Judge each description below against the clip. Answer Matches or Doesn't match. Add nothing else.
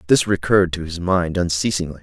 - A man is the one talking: Matches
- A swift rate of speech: Doesn't match